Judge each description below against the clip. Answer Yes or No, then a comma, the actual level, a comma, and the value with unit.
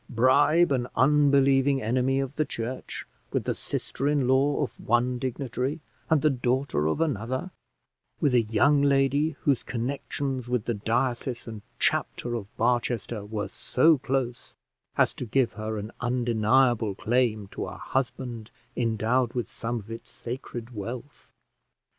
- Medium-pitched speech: No, low, 125 Hz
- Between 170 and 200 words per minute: No, average, 145 wpm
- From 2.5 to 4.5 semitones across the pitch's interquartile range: Yes, average, 2.9 semitones